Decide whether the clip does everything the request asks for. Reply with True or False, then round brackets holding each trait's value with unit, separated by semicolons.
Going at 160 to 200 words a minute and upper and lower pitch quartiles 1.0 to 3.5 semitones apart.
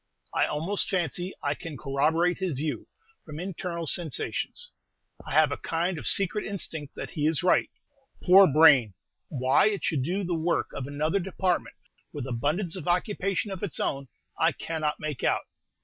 False (165 wpm; 3.9 semitones)